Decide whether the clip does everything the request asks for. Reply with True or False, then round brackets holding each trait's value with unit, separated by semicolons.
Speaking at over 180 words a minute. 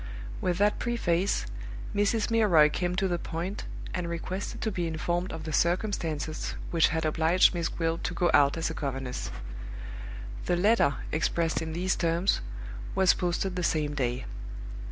False (155 wpm)